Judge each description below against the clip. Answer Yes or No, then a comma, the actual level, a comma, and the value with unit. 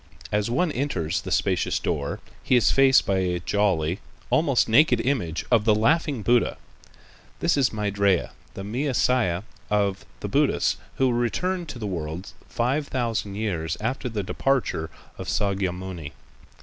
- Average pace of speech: Yes, average, 150 wpm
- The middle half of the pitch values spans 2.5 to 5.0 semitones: No, wide, 5.4 semitones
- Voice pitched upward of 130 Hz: No, low, 110 Hz